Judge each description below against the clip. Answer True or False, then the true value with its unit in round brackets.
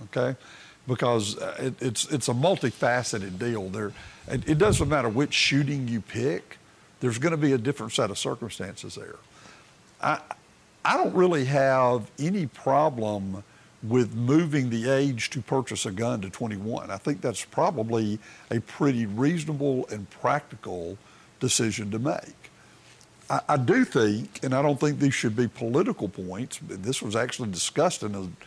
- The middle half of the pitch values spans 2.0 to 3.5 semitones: False (4.2 semitones)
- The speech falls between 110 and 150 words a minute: False (160 wpm)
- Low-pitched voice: True (125 Hz)